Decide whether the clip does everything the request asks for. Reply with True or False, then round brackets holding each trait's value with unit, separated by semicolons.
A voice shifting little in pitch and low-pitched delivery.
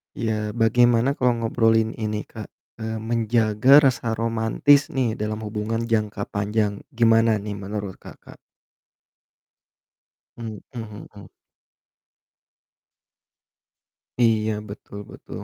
True (1.6 semitones; 110 Hz)